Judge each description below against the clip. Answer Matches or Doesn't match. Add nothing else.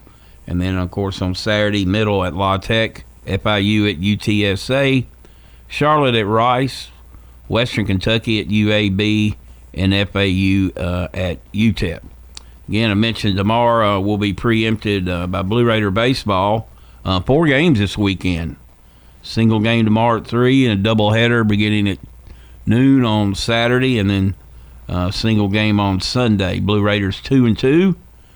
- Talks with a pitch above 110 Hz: Doesn't match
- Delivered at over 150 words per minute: Doesn't match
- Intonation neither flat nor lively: Matches